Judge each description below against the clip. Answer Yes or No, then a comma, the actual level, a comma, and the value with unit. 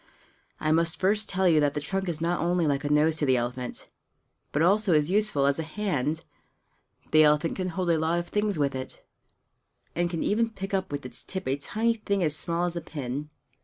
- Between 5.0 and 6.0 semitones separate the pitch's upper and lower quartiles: No, average, 4.3 semitones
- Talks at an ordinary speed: No, fast, 220 wpm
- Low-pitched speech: No, medium, 165 Hz